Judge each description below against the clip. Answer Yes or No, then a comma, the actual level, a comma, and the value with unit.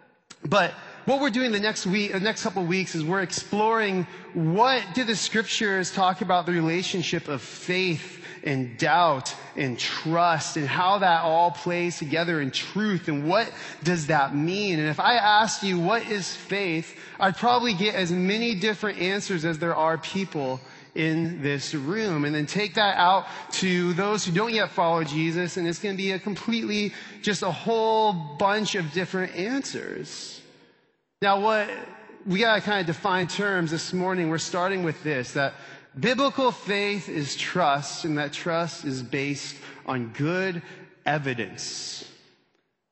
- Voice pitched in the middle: Yes, medium, 180 Hz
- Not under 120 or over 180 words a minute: Yes, average, 165 wpm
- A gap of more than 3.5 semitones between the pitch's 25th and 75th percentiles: Yes, average, 4.0 semitones